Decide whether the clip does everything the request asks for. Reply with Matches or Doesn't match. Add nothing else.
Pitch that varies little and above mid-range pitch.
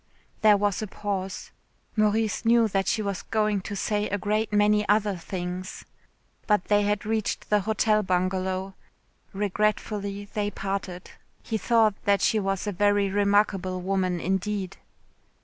Matches